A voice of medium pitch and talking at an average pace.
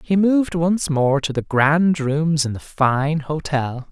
Yes: medium, 150 Hz; average, 185 wpm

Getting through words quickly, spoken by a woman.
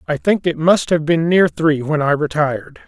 No: fast, 230 wpm; male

